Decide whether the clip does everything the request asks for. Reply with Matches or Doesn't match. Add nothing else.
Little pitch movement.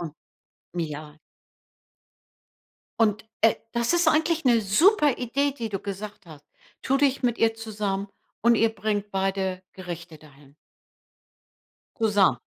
Doesn't match